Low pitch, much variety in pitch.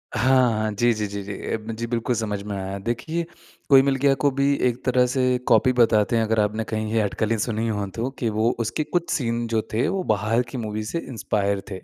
No: low, 115 Hz; average, 2.8 semitones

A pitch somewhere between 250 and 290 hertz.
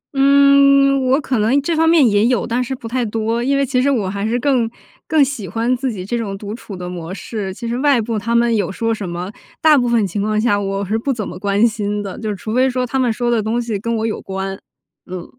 No: high, 230 Hz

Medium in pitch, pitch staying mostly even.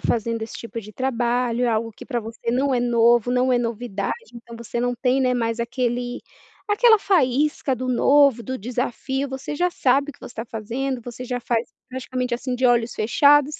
No: high, 245 Hz; narrow, 2.2 semitones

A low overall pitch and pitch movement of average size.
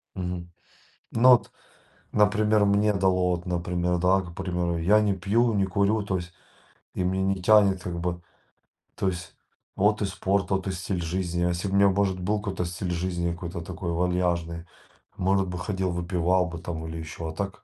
No: very low, 90 Hz; narrow, 2.1 semitones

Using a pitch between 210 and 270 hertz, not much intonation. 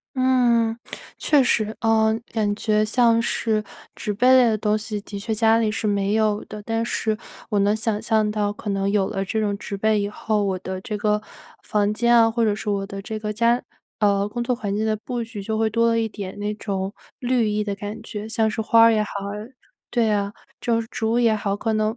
Yes: high, 215 Hz; narrow, 1.7 semitones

